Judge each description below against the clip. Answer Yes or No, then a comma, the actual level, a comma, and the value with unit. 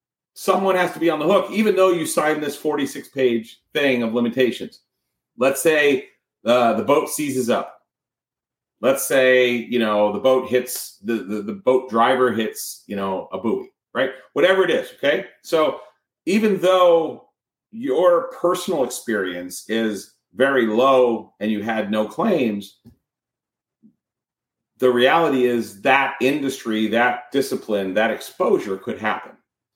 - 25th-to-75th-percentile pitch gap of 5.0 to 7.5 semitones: Yes, wide, 5.4 semitones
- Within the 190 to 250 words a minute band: No, average, 140 wpm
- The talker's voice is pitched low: Yes, low, 125 Hz